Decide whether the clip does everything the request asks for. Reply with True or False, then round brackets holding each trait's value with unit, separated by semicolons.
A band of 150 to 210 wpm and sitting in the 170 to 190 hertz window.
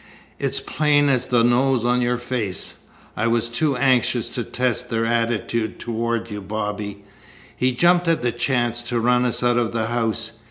False (175 wpm; 120 Hz)